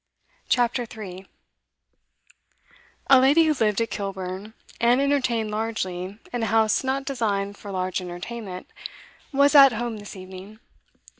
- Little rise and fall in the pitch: No, average, 4.1 semitones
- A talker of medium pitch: No, high, 220 Hz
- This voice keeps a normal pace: No, slow, 130 wpm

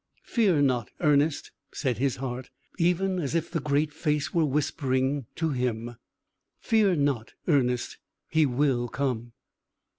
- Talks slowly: Yes, slow, 125 wpm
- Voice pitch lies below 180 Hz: Yes, medium, 140 Hz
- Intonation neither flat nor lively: Yes, average, 3.9 semitones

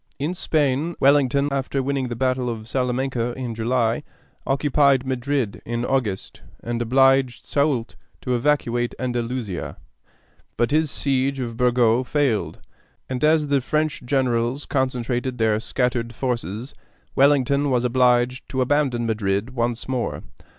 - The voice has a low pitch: Yes, low, 130 Hz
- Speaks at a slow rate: Yes, slow, 130 wpm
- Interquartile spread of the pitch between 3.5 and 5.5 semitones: No, narrow, 2.5 semitones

